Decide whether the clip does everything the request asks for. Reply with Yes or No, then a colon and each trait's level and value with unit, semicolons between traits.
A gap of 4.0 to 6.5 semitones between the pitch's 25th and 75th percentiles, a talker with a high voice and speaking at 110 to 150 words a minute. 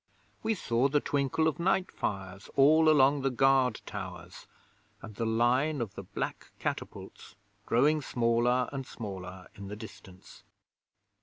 No: average, 4.9 semitones; low, 125 Hz; average, 140 wpm